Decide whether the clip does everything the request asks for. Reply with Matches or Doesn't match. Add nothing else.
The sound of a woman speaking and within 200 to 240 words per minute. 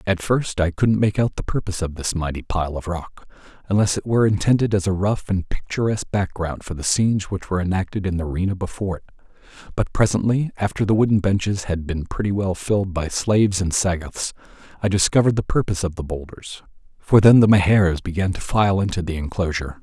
Doesn't match